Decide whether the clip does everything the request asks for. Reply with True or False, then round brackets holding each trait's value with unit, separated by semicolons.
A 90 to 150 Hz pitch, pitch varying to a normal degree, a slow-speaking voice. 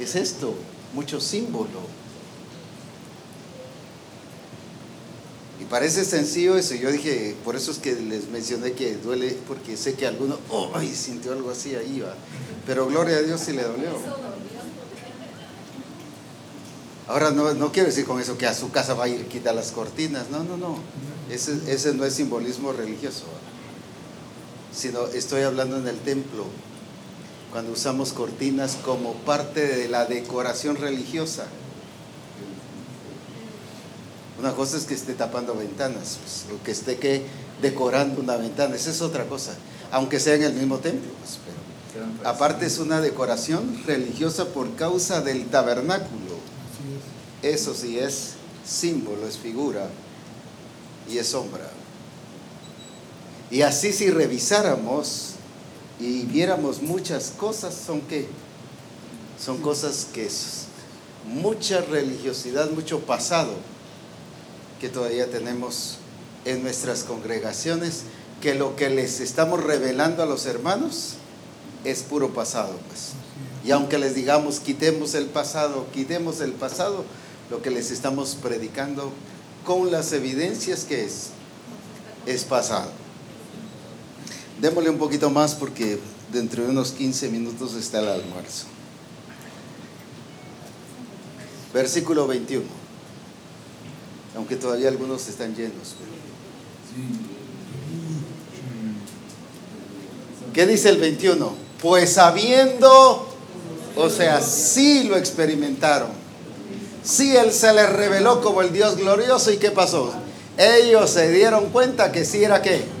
True (140 Hz; 4.4 semitones; 125 wpm)